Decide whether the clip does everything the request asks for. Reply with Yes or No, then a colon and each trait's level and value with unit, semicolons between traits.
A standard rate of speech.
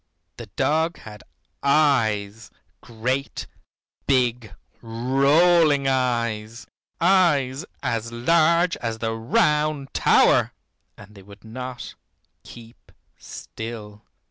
No: slow, 90 wpm